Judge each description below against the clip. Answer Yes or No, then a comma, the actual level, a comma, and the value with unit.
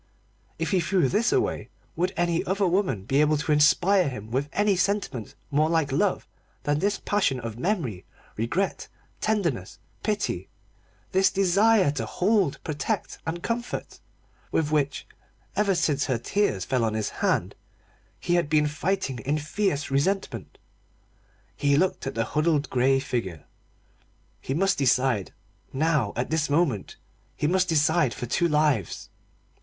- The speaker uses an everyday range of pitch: No, wide, 5.8 semitones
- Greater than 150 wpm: No, average, 145 wpm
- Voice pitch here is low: No, medium, 150 Hz